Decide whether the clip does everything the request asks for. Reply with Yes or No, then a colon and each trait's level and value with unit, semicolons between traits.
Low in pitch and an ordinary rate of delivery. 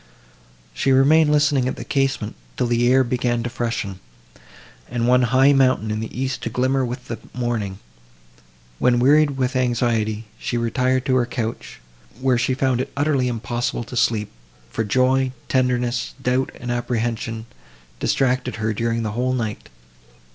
Yes: low, 125 Hz; average, 155 wpm